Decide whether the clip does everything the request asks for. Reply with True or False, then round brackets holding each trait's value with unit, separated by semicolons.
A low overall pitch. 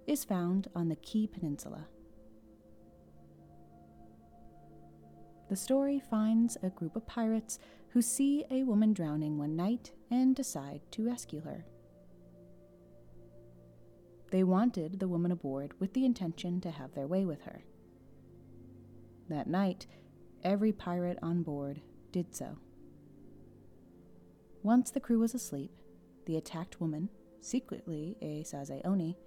False (170 Hz)